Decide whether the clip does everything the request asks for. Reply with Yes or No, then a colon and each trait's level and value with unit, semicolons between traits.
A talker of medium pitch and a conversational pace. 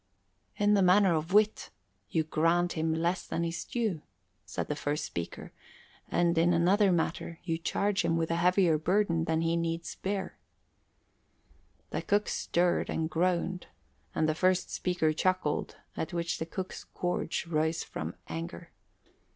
Yes: medium, 170 Hz; average, 150 wpm